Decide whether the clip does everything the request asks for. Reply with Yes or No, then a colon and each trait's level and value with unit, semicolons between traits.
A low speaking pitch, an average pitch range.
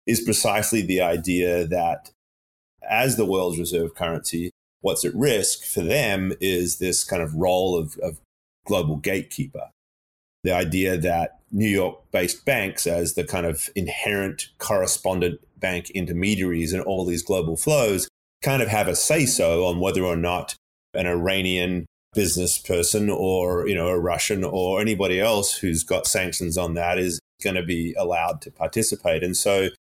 No: very low, 90 Hz; narrow, 1.8 semitones